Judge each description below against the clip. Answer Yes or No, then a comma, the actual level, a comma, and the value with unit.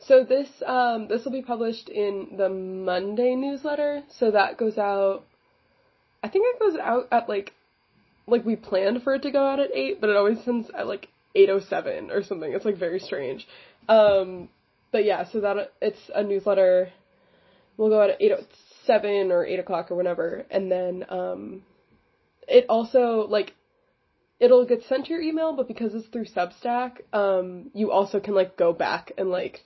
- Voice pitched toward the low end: No, high, 215 Hz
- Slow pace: No, average, 190 wpm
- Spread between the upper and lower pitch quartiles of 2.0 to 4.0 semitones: No, average, 5.3 semitones